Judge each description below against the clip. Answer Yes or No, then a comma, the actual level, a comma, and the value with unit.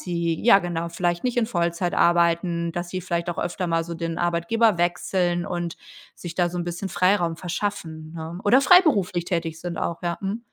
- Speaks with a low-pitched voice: No, medium, 175 Hz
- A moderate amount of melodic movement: No, narrow, 1.6 semitones